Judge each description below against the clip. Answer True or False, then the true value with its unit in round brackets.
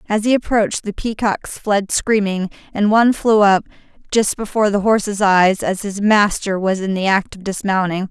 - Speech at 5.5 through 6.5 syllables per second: False (5.0 syllables/s)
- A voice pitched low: False (200 Hz)